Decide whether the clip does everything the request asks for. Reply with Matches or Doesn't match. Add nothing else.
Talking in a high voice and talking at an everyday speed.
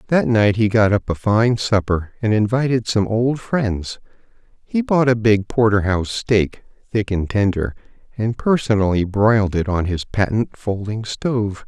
Doesn't match